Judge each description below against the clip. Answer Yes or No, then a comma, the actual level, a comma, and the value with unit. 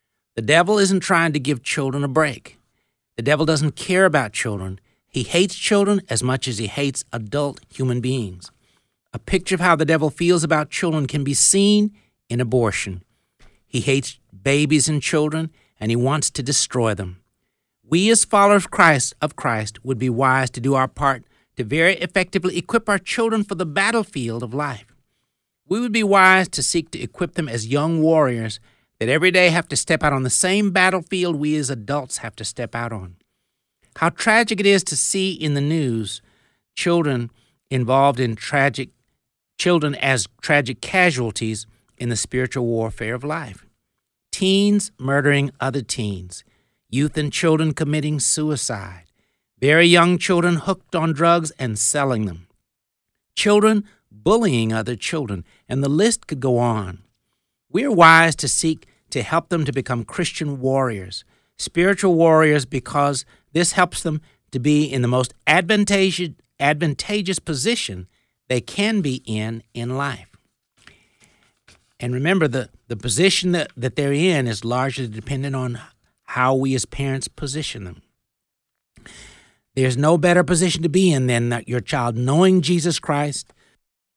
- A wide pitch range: Yes, wide, 6.0 semitones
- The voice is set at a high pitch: No, medium, 140 Hz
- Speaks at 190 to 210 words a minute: No, average, 160 wpm